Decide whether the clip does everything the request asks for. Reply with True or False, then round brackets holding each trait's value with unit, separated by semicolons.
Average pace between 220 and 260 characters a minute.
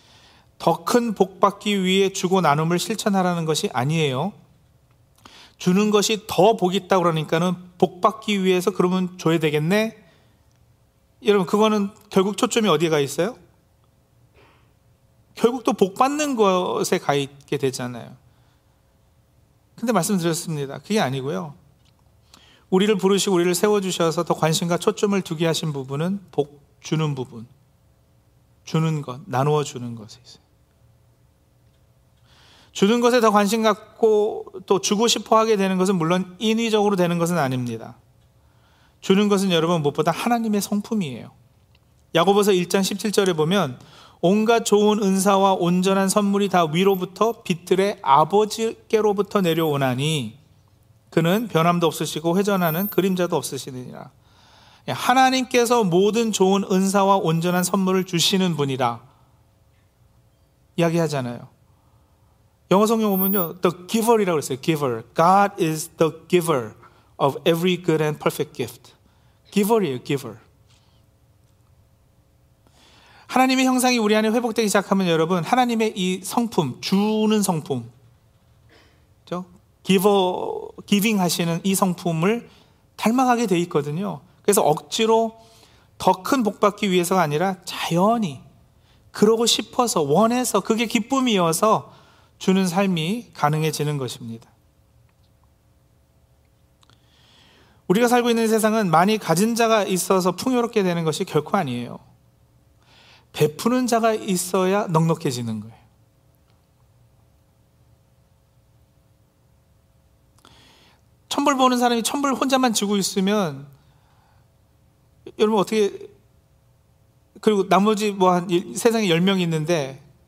False (285 characters per minute)